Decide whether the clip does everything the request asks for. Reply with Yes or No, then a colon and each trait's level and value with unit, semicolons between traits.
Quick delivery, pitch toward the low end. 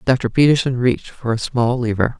No: average, 190 wpm; low, 125 Hz